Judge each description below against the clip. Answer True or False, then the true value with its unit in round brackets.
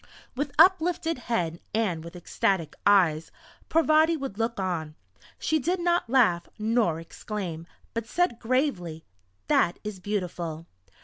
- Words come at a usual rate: False (125 wpm)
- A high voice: True (210 Hz)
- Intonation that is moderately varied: False (8.5 semitones)